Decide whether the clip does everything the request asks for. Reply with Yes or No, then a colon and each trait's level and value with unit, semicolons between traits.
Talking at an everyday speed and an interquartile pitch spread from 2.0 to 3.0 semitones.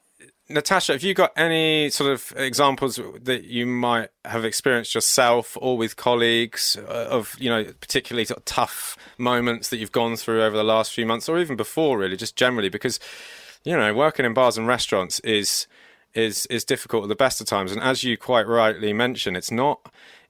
Yes: average, 185 wpm; average, 2.7 semitones